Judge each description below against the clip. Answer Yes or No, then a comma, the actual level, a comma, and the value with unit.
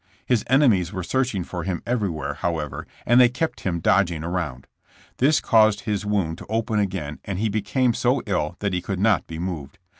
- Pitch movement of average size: Yes, average, 4.6 semitones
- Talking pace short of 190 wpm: No, average, 200 wpm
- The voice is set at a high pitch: No, low, 100 Hz